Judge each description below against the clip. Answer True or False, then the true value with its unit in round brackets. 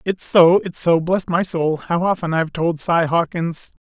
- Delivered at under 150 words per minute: False (205 wpm)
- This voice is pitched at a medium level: True (170 Hz)